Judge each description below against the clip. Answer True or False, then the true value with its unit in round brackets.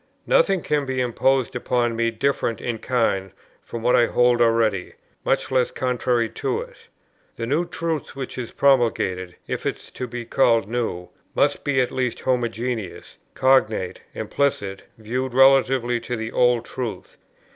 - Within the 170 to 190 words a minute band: False (155 wpm)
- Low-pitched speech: True (120 Hz)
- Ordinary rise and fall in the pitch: False (2.3 semitones)